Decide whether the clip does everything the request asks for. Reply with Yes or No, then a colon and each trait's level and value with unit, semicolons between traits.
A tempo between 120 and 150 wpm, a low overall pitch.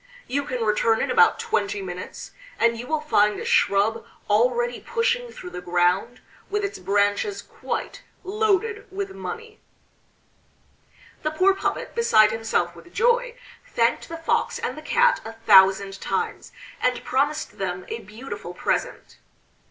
No: average, 145 wpm; high, 240 Hz